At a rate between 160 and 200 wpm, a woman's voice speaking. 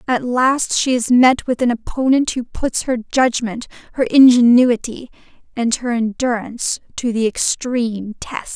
No: average, 145 wpm; female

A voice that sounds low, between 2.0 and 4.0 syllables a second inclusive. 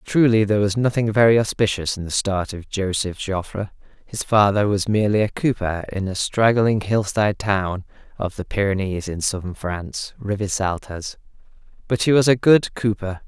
No: low, 105 Hz; 5.1 syllables/s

